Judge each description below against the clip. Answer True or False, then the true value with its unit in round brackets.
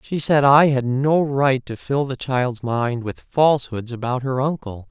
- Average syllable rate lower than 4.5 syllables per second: True (4.2 syllables/s)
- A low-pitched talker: True (130 Hz)